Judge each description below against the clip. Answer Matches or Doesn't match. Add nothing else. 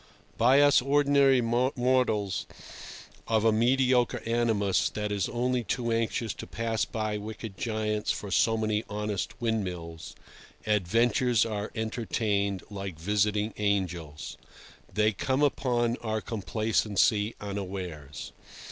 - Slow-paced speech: Matches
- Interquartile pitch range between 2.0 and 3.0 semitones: Matches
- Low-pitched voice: Matches